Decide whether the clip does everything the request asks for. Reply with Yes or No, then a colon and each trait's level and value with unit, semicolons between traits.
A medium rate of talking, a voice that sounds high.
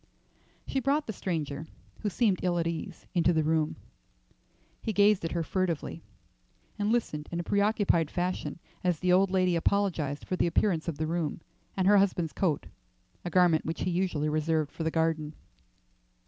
No: average, 175 wpm; medium, 175 Hz